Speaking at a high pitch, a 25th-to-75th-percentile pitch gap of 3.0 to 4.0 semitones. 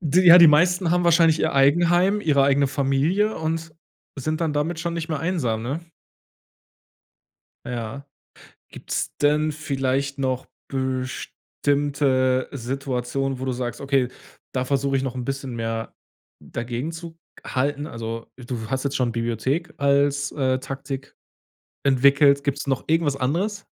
No: medium, 140 Hz; average, 3.3 semitones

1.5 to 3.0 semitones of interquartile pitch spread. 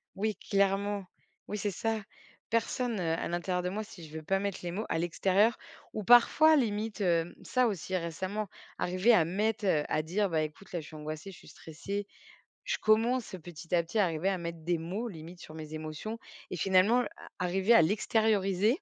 No: average, 4.2 semitones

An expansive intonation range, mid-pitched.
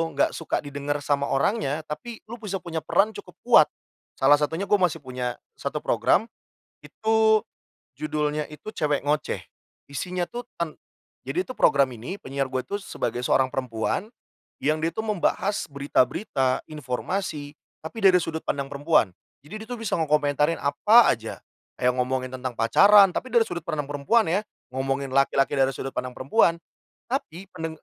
Yes: wide, 6.0 semitones; medium, 150 Hz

